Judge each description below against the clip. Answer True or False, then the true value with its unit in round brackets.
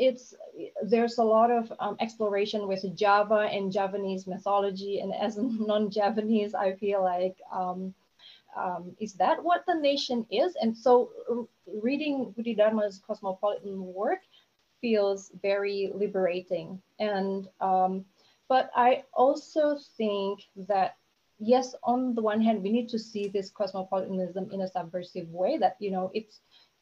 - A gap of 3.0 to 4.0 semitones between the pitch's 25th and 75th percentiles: True (3.4 semitones)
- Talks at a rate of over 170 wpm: False (140 wpm)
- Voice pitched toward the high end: True (205 Hz)